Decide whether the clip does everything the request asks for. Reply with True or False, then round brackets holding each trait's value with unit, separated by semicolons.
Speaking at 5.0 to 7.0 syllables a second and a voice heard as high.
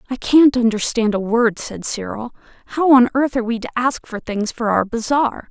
True (5.1 syllables/s; 235 Hz)